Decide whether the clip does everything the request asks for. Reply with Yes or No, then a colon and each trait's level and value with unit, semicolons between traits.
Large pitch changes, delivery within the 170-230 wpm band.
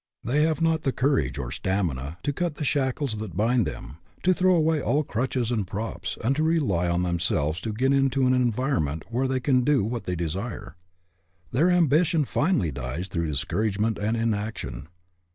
Yes: wide, 7.8 semitones; average, 190 wpm